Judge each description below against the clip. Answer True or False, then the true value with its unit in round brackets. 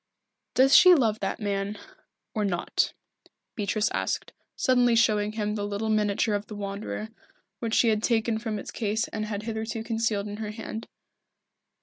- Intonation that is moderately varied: False (1.5 semitones)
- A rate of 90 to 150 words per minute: False (160 wpm)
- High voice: True (215 Hz)